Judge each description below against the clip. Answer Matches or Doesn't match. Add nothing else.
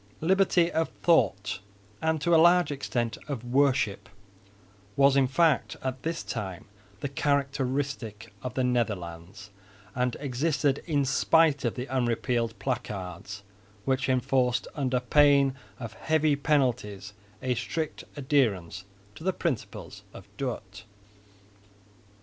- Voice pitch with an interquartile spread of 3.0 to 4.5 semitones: Matches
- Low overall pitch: Matches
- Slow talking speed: Matches